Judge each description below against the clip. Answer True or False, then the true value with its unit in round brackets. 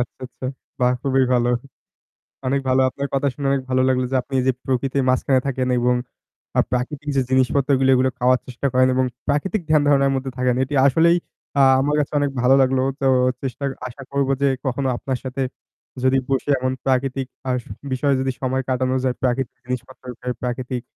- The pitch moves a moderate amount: False (1.4 semitones)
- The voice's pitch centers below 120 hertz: False (130 Hz)